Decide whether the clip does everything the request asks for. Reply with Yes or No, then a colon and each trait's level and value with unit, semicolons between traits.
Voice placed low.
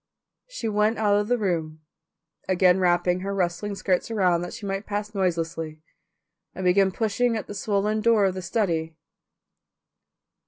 No: high, 195 Hz